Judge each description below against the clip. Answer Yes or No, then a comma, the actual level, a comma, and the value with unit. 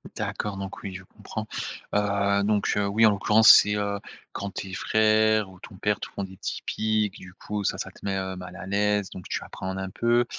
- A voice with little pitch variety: Yes, narrow, 1.6 semitones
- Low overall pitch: Yes, low, 100 Hz